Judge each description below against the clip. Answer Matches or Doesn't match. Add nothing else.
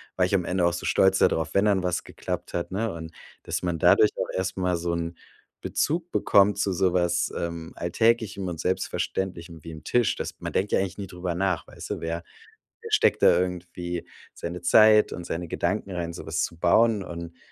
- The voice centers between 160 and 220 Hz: Doesn't match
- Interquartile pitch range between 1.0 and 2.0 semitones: Doesn't match